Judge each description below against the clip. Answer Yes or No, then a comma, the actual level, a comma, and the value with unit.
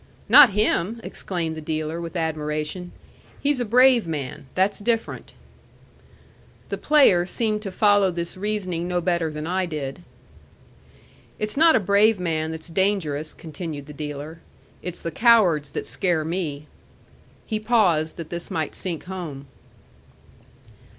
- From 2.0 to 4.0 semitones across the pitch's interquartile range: No, average, 4.6 semitones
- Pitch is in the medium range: Yes, medium, 175 Hz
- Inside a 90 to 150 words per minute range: Yes, slow, 135 wpm